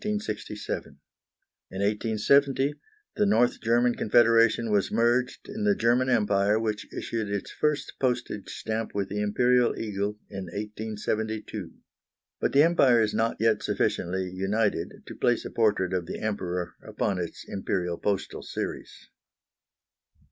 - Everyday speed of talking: No, slow, 130 wpm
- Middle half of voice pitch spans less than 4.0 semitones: Yes, average, 3.2 semitones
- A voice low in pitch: Yes, low, 110 Hz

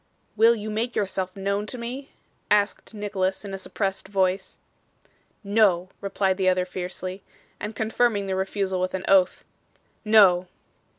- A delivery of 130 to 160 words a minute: Yes, average, 140 wpm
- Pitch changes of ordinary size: No, narrow, 2.2 semitones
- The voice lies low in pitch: No, high, 195 Hz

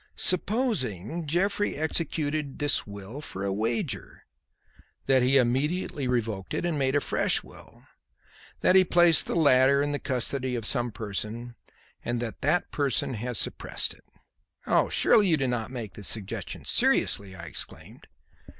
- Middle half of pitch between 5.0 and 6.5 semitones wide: Yes, average, 5.3 semitones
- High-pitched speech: No, low, 130 Hz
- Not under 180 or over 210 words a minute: No, average, 150 wpm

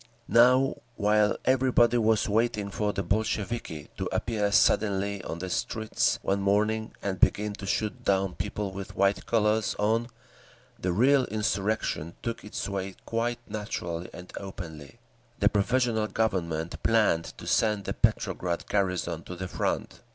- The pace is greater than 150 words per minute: No, average, 145 wpm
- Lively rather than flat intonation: No, narrow, 2.6 semitones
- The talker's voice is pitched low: Yes, low, 105 Hz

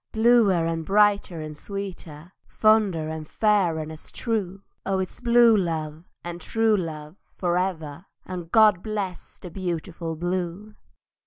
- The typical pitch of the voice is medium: Yes, medium, 180 Hz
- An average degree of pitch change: Yes, average, 4.0 semitones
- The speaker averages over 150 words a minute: No, average, 140 wpm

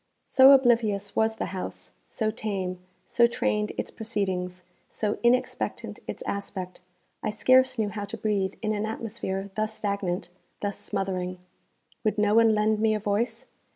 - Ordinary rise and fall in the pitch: No, narrow, 2.1 semitones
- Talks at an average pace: Yes, average, 155 wpm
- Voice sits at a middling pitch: No, high, 210 Hz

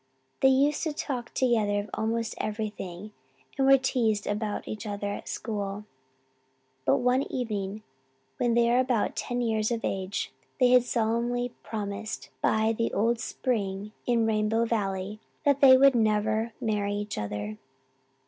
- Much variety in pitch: No, average, 2.9 semitones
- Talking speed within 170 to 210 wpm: No, average, 150 wpm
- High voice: Yes, high, 220 Hz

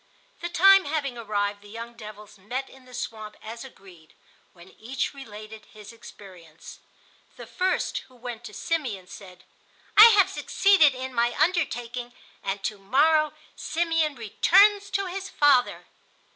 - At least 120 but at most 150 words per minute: Yes, average, 145 wpm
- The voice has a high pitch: Yes, high, 245 Hz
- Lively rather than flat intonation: Yes, wide, 6.9 semitones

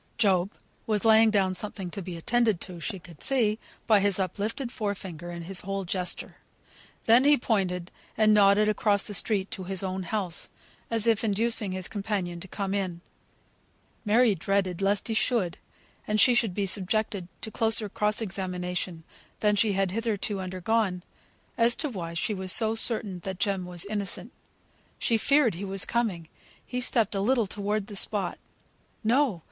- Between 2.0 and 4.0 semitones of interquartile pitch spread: Yes, average, 3.0 semitones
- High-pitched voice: Yes, high, 200 Hz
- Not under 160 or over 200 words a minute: Yes, average, 175 wpm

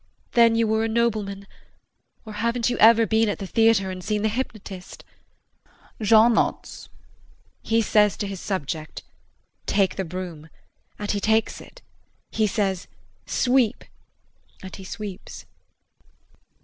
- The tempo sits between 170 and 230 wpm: No, slow, 135 wpm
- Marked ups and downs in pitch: No, narrow, 2.6 semitones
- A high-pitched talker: Yes, high, 210 Hz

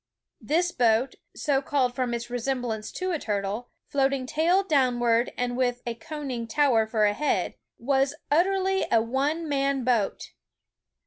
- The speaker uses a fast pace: No, average, 150 wpm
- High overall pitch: Yes, very high, 260 Hz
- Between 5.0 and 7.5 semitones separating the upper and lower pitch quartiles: No, average, 3.7 semitones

